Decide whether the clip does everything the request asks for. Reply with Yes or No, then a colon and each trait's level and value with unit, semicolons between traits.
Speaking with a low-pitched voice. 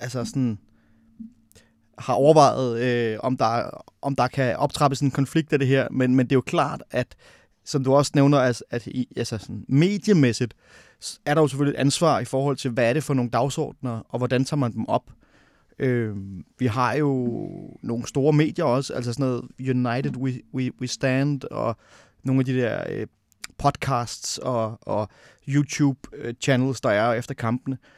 Yes: low, 130 Hz